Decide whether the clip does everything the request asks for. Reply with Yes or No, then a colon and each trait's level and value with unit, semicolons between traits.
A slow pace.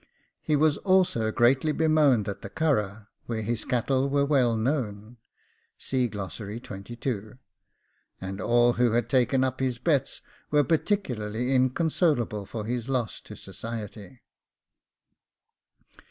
Yes: slow, 110 wpm